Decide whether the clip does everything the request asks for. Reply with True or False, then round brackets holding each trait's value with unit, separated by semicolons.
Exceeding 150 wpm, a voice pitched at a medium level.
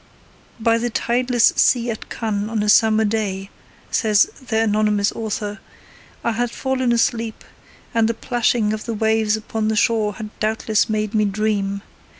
False (160 wpm; 220 Hz)